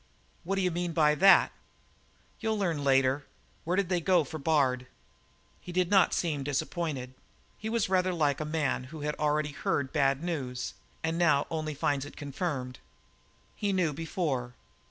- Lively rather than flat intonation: No, average, 4.1 semitones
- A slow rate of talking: No, average, 160 wpm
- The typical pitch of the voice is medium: Yes, medium, 155 Hz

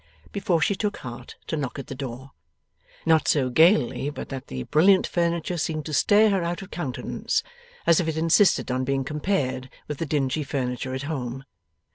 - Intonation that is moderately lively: Yes, average, 4.5 semitones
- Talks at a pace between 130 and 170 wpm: No, average, 185 wpm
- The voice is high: No, medium, 150 Hz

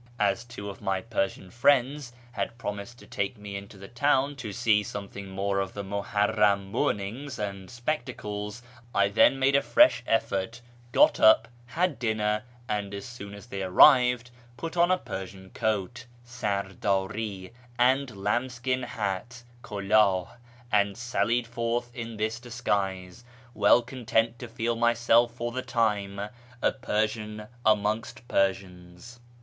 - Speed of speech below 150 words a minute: Yes, average, 140 wpm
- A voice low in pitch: Yes, low, 110 Hz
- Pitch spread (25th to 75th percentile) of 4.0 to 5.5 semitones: No, average, 3.4 semitones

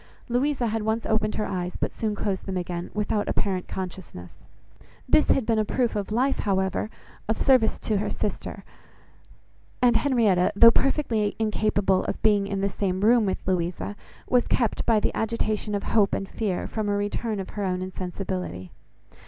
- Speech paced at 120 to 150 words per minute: No, average, 175 wpm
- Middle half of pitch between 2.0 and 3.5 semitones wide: Yes, average, 2.9 semitones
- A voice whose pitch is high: Yes, high, 210 Hz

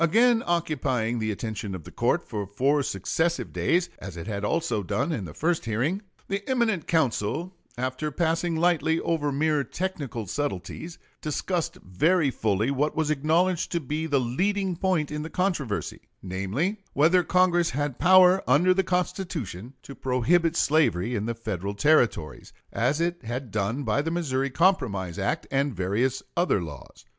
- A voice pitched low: No, medium, 145 Hz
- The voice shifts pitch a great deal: Yes, wide, 7.3 semitones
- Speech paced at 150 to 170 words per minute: Yes, average, 160 wpm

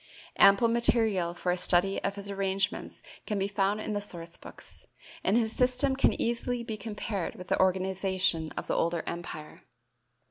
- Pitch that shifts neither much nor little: Yes, average, 3.4 semitones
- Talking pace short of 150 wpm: No, average, 170 wpm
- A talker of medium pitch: No, high, 195 Hz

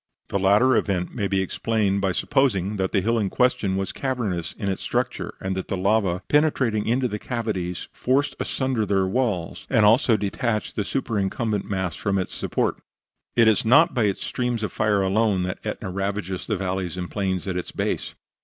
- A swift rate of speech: No, average, 190 wpm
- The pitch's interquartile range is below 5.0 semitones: Yes, average, 3.4 semitones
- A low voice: Yes, low, 100 Hz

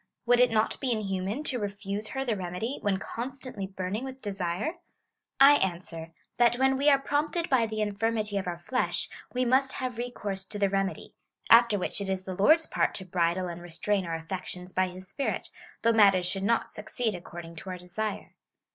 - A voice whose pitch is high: Yes, high, 205 Hz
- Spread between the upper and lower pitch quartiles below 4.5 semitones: No, average, 4.8 semitones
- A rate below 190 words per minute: No, average, 195 wpm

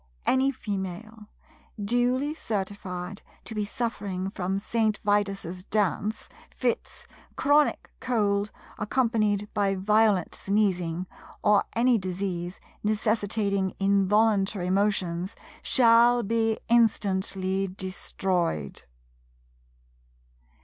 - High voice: Yes, high, 205 Hz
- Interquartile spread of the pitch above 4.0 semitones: No, average, 2.8 semitones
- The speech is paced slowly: Yes, slow, 80 wpm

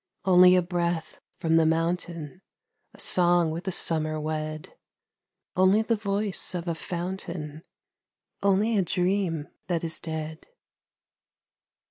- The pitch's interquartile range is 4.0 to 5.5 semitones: No, average, 2.8 semitones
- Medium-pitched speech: Yes, medium, 175 Hz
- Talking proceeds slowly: Yes, slow, 120 wpm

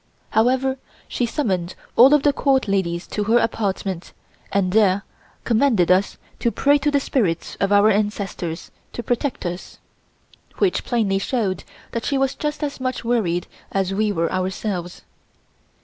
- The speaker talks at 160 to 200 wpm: No, average, 150 wpm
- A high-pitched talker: Yes, high, 215 Hz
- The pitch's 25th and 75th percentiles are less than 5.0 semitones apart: No, wide, 5.4 semitones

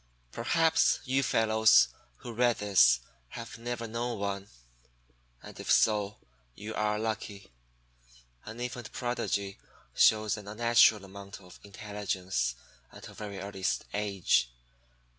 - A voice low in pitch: Yes, low, 105 Hz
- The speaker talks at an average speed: No, slow, 120 wpm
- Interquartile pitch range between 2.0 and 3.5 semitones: Yes, average, 2.8 semitones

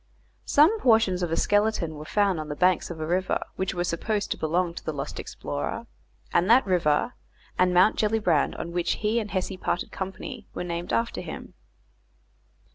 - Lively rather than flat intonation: No, average, 3.9 semitones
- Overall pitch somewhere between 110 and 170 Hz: No, medium, 185 Hz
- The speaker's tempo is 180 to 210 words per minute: Yes, average, 185 wpm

